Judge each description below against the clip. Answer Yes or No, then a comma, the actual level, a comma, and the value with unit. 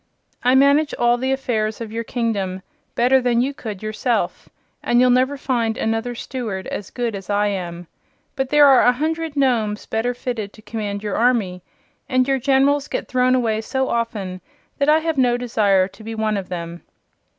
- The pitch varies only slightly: No, average, 3.7 semitones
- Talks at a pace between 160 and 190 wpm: Yes, average, 185 wpm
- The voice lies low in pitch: No, high, 235 Hz